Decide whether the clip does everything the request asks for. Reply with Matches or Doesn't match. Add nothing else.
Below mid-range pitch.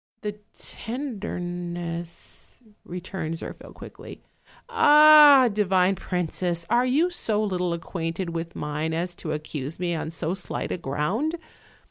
Doesn't match